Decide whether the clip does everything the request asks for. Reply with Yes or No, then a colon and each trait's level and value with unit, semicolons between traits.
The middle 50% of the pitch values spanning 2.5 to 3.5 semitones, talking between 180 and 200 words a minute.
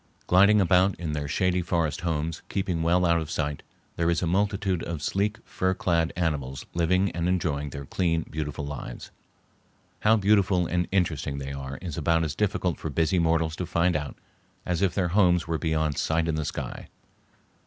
Yes: average, 2.9 semitones; average, 185 wpm